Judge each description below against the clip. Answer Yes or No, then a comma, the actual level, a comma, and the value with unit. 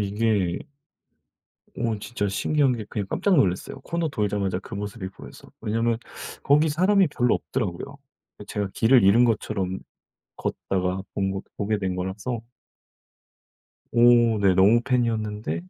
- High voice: No, low, 110 Hz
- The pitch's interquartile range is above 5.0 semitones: No, average, 3.7 semitones